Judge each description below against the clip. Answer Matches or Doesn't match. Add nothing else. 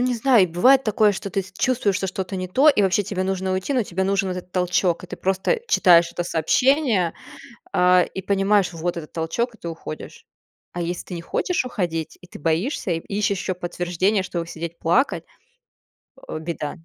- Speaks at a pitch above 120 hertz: Matches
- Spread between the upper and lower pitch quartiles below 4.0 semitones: Matches